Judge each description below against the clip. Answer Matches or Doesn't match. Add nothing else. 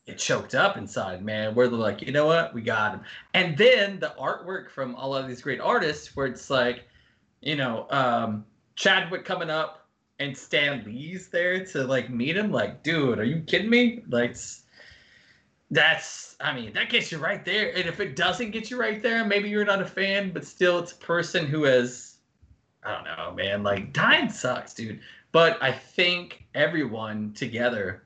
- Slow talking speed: Doesn't match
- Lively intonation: Matches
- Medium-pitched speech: Matches